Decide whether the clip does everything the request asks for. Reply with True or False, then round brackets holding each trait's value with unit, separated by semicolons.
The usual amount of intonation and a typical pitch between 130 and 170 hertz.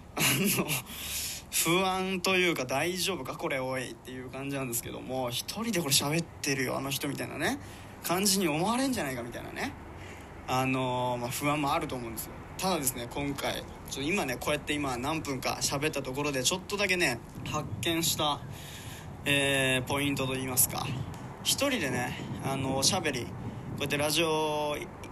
True (3.8 semitones; 140 Hz)